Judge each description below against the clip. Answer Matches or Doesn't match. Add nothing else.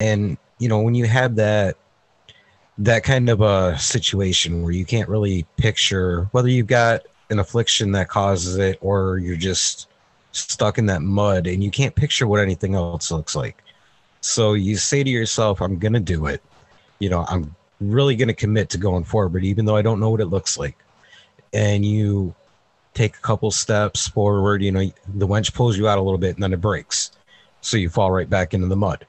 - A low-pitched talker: Matches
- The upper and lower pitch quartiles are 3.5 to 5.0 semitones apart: Doesn't match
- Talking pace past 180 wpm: Matches